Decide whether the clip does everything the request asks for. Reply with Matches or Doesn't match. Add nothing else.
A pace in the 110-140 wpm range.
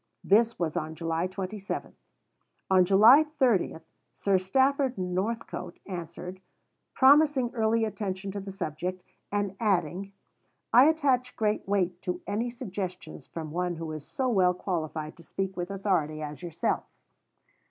Matches